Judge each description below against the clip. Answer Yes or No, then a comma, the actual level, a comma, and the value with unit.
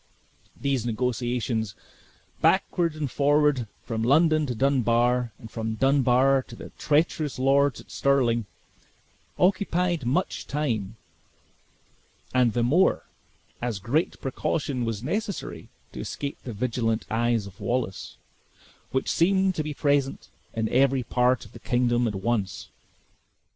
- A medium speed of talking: No, slow, 125 wpm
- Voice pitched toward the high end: No, low, 125 Hz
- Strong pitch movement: No, average, 3.7 semitones